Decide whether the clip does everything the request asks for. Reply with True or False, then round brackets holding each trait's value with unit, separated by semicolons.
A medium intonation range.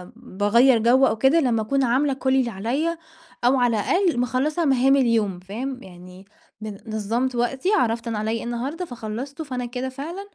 True (3.3 semitones)